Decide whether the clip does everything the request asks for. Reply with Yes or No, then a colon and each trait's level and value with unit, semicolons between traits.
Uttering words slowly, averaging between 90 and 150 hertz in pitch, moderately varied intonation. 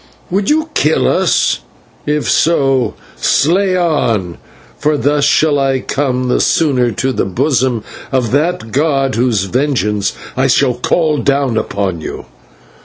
Yes: slow, 130 wpm; low, 135 Hz; average, 3.7 semitones